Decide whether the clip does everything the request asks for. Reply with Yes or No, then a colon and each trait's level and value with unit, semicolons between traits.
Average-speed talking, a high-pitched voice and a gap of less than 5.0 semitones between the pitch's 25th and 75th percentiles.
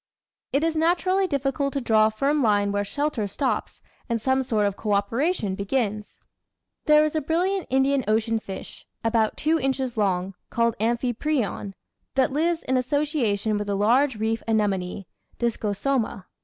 No: average, 155 wpm; high, 235 Hz; wide, 5.4 semitones